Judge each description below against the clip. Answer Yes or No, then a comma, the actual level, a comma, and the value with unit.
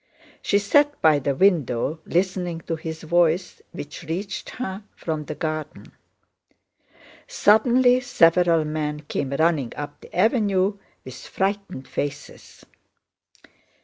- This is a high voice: No, medium, 170 Hz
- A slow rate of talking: Yes, slow, 115 wpm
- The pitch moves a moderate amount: Yes, average, 4.7 semitones